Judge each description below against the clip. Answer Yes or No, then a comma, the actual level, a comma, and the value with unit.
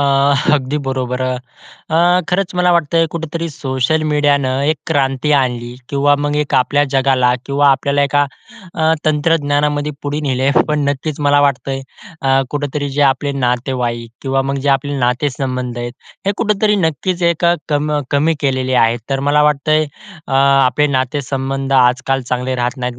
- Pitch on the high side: No, medium, 140 Hz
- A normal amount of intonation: No, narrow, 2.2 semitones